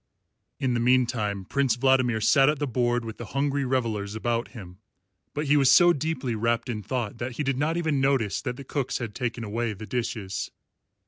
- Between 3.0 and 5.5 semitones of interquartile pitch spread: Yes, average, 3.4 semitones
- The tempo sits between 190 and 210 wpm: Yes, average, 200 wpm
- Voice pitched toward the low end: Yes, low, 125 Hz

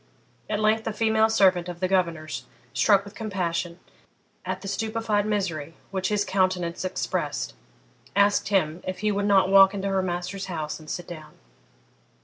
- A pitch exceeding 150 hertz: Yes, high, 190 Hz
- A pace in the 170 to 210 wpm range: No, average, 160 wpm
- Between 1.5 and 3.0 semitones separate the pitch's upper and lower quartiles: Yes, average, 2.7 semitones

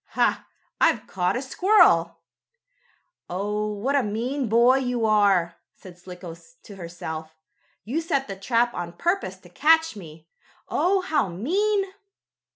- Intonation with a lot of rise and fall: Yes, wide, 8.0 semitones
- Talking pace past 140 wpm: No, slow, 135 wpm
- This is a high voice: Yes, high, 215 Hz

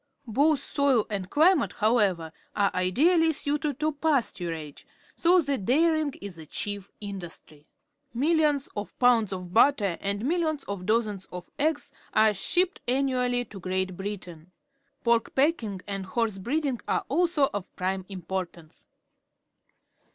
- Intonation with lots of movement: Yes, wide, 7.2 semitones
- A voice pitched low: No, high, 225 Hz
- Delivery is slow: Yes, slow, 130 wpm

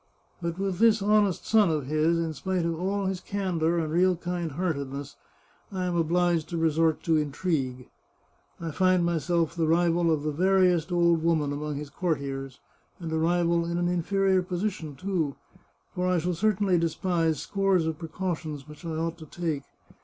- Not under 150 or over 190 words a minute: Yes, average, 175 wpm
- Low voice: No, medium, 170 Hz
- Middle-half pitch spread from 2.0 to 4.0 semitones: Yes, narrow, 2.5 semitones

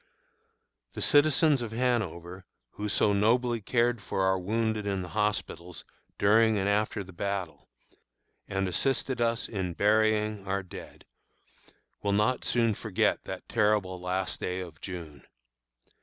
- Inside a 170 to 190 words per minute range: No, slow, 135 wpm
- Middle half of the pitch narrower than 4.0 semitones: Yes, average, 3.3 semitones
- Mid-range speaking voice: No, low, 105 Hz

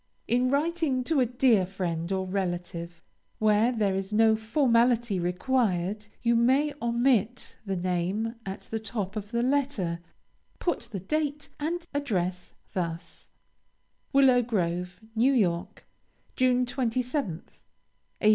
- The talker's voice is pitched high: Yes, high, 225 Hz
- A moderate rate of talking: No, slow, 125 wpm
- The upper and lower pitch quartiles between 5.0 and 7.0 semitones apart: Yes, wide, 5.4 semitones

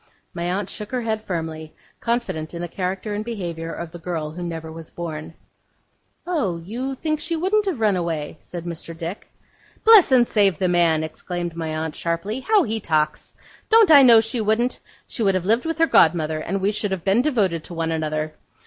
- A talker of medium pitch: Yes, medium, 180 Hz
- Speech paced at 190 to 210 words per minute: Yes, fast, 205 wpm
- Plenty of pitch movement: Yes, wide, 5.9 semitones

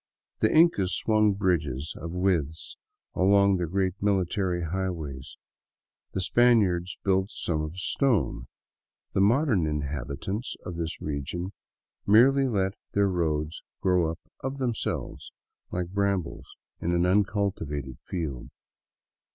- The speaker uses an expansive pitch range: No, average, 3.9 semitones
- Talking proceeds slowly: Yes, slow, 115 wpm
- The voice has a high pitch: No, very low, 90 Hz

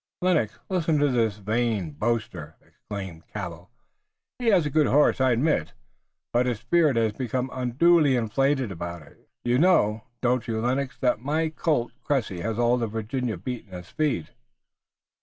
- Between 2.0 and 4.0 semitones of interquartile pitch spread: No, average, 4.6 semitones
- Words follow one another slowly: No, average, 155 wpm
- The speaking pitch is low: Yes, low, 120 Hz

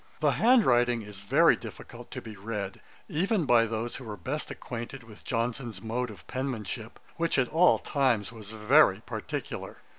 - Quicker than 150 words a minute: Yes, average, 170 wpm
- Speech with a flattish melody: No, average, 3.5 semitones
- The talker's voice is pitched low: Yes, low, 120 Hz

